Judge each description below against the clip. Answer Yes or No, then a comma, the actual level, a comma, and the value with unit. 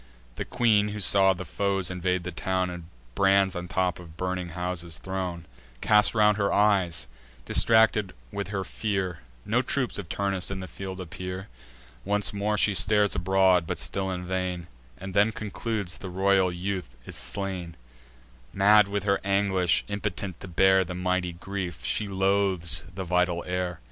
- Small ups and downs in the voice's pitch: Yes, narrow, 1.9 semitones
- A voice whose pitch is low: Yes, very low, 95 Hz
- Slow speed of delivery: No, average, 165 wpm